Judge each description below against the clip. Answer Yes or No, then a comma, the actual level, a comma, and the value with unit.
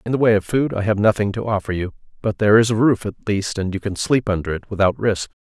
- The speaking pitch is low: Yes, low, 105 Hz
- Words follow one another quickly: Yes, fast, 285 wpm